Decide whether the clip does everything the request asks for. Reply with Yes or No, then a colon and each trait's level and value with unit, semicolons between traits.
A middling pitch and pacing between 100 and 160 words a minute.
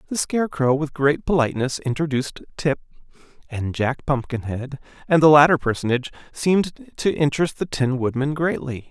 Yes: medium, 145 Hz; average, 140 wpm